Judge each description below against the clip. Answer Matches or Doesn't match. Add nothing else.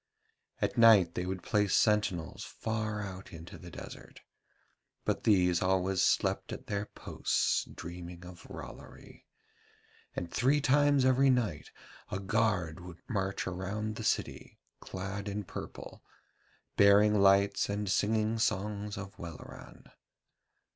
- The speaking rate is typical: Doesn't match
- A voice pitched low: Matches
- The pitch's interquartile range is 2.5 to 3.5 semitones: Matches